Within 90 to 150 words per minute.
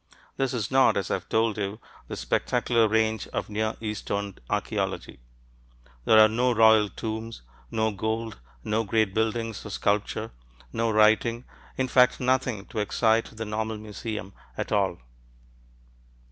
Yes: average, 140 wpm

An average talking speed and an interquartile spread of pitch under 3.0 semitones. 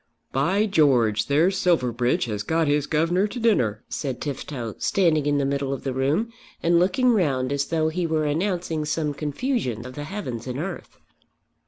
No: average, 175 wpm; average, 5.0 semitones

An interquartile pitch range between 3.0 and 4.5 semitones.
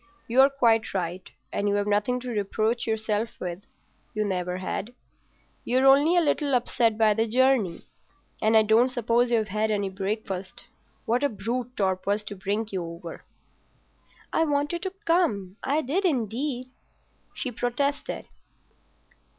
Yes: average, 4.1 semitones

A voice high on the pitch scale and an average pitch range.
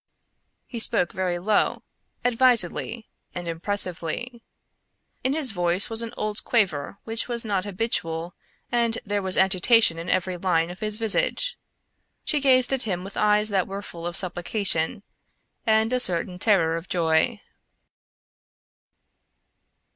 Yes: high, 200 Hz; average, 4.5 semitones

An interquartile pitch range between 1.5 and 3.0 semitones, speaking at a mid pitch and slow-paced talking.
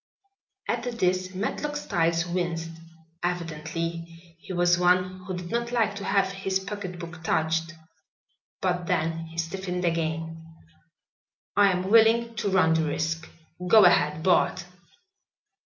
Yes: average, 2.7 semitones; medium, 180 Hz; slow, 125 wpm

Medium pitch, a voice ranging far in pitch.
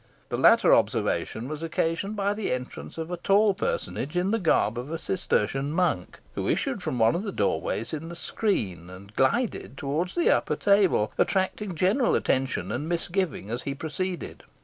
Yes: medium, 165 Hz; wide, 6.8 semitones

